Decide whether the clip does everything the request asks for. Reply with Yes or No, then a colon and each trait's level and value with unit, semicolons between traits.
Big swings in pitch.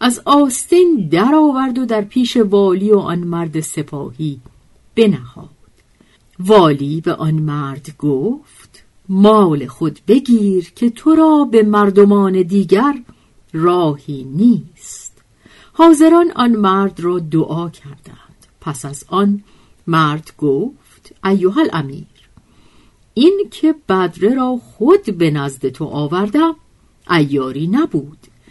Yes: wide, 7.3 semitones